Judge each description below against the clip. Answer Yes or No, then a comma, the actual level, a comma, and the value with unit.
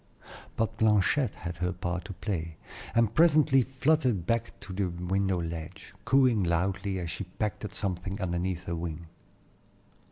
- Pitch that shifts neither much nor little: Yes, average, 4.2 semitones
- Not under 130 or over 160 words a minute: Yes, average, 150 wpm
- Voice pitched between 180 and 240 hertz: No, very low, 95 Hz